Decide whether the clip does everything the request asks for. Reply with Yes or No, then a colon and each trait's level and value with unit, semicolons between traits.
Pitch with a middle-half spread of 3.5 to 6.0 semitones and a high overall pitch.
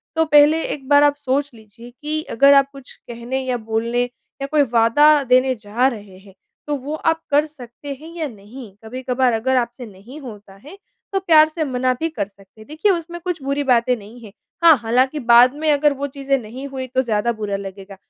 Yes: average, 4.1 semitones; very high, 260 Hz